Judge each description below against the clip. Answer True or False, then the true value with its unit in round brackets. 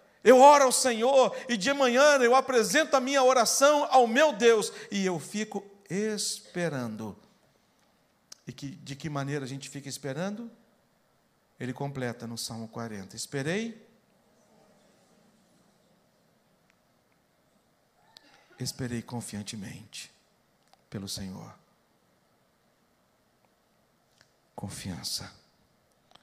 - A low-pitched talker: False (205 Hz)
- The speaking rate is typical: False (90 wpm)